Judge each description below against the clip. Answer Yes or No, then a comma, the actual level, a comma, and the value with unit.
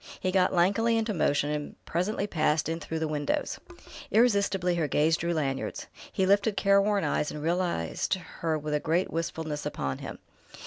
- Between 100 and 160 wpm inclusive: No, average, 170 wpm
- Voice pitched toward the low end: No, medium, 170 Hz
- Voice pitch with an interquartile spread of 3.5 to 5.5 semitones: Yes, average, 4.5 semitones